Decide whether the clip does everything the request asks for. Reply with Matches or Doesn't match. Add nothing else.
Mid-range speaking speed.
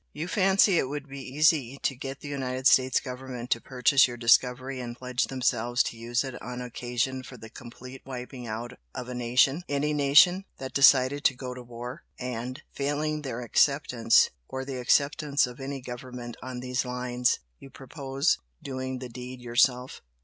Matches